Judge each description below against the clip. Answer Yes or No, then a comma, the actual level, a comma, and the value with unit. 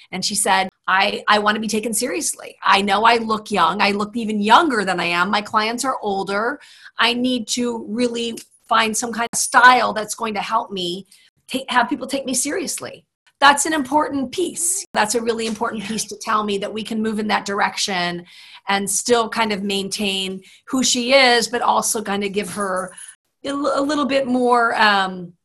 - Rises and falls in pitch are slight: No, average, 3.5 semitones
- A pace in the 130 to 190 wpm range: No, average, 200 wpm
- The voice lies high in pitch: Yes, high, 220 Hz